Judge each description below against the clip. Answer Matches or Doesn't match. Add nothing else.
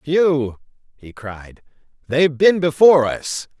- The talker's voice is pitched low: Doesn't match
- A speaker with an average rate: Doesn't match